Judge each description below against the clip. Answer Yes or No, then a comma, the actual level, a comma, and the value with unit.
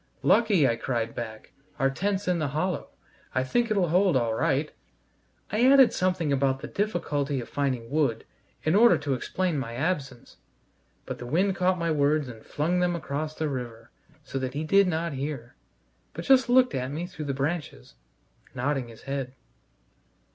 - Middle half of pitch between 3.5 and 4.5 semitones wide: No, wide, 5.5 semitones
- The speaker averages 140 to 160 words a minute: No, average, 175 wpm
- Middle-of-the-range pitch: Yes, medium, 145 Hz